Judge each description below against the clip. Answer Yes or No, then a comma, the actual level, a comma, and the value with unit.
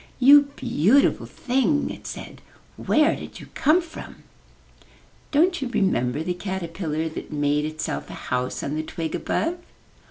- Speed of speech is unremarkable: Yes, average, 145 wpm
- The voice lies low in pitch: No, high, 190 Hz